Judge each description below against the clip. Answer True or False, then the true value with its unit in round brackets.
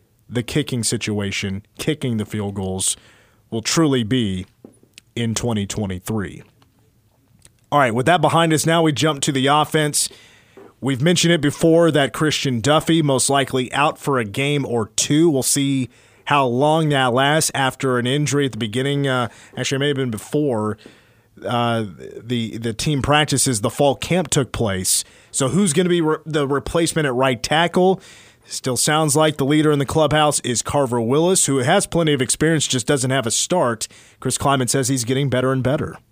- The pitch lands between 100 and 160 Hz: True (135 Hz)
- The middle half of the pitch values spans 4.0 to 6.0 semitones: True (4.5 semitones)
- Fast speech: False (180 wpm)